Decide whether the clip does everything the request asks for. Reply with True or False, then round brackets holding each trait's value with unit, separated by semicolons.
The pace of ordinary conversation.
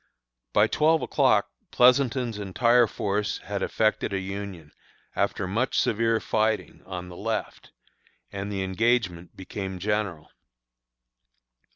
False (110 wpm)